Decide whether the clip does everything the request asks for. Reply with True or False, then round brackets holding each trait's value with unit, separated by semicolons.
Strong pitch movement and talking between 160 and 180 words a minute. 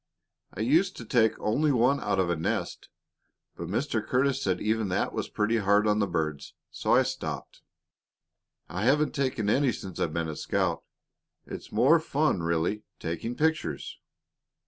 True (6.7 semitones; 165 wpm)